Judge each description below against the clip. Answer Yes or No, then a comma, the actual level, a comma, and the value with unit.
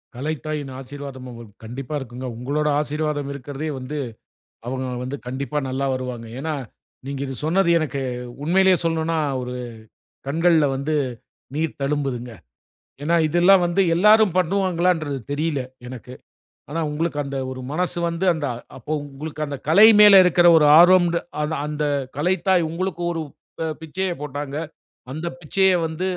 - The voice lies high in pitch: No, medium, 150 Hz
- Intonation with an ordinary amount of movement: Yes, average, 3.9 semitones